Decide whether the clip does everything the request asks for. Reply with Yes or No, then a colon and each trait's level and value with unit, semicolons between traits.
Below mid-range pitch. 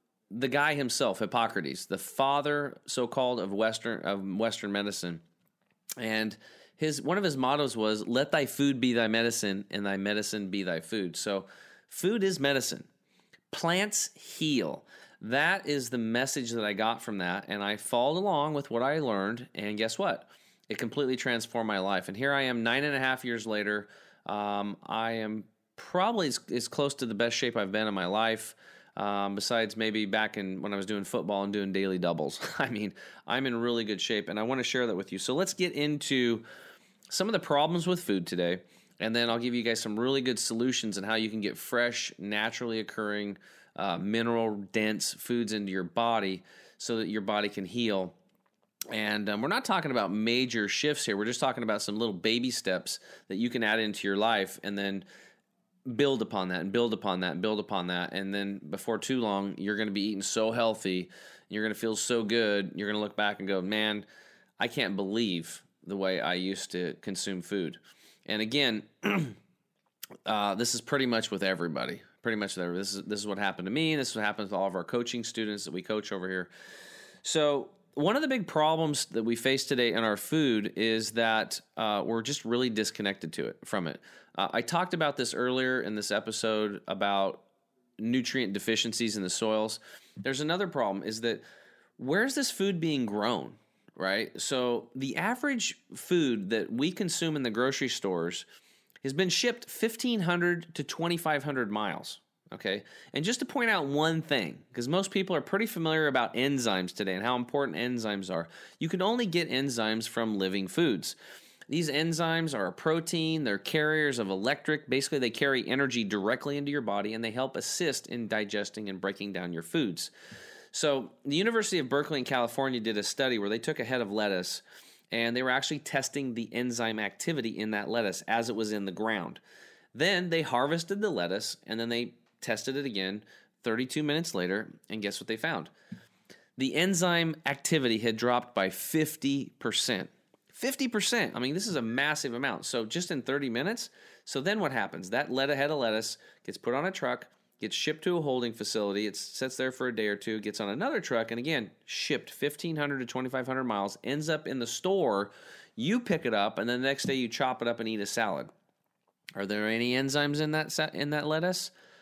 Yes: low, 115 Hz